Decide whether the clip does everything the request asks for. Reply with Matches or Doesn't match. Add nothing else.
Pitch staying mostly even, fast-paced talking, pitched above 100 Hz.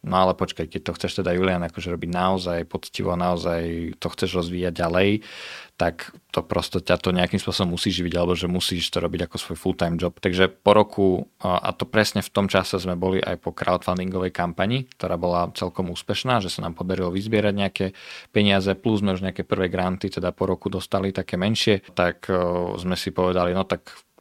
Doesn't match